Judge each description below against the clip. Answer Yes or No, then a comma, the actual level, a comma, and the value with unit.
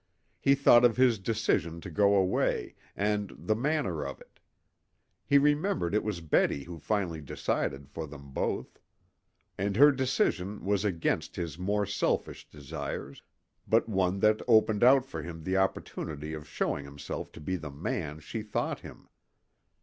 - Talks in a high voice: No, very low, 95 Hz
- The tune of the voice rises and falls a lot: Yes, wide, 5.7 semitones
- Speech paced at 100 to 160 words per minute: Yes, average, 155 wpm